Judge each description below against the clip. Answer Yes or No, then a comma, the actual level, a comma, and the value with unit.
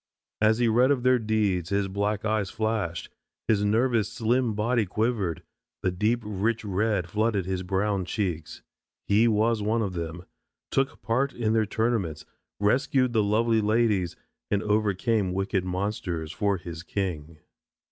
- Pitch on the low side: Yes, low, 105 Hz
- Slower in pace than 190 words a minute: Yes, average, 145 wpm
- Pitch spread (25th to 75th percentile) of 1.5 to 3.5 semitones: Yes, average, 3.1 semitones